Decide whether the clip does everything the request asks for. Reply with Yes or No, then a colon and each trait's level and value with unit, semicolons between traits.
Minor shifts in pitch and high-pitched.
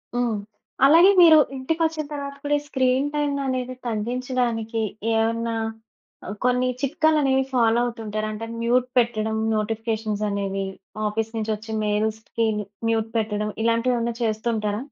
No: average, 3.0 semitones; high, 230 Hz